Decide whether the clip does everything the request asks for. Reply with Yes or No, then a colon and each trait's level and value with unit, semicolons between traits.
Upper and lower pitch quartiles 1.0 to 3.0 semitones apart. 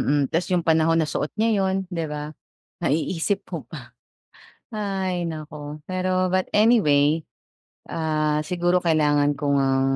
No: average, 3.7 semitones